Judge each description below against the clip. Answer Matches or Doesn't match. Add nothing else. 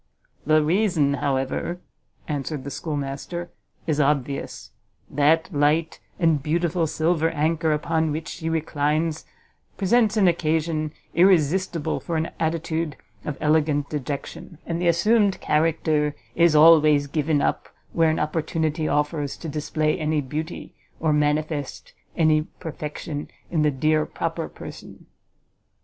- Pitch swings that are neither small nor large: Doesn't match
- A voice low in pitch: Doesn't match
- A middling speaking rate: Doesn't match